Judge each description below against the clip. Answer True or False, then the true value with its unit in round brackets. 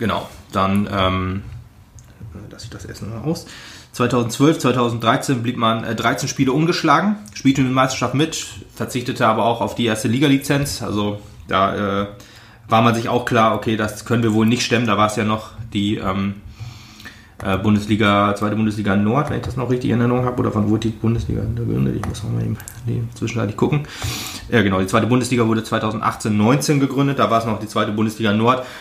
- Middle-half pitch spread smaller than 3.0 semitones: True (2.6 semitones)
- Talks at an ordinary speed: False (195 wpm)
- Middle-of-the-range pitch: False (115 Hz)